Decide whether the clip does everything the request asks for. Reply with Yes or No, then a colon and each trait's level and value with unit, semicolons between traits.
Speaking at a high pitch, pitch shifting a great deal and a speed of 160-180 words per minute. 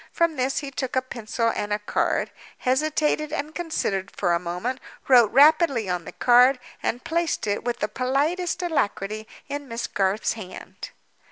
No: very high, 255 Hz; wide, 6.0 semitones; average, 150 wpm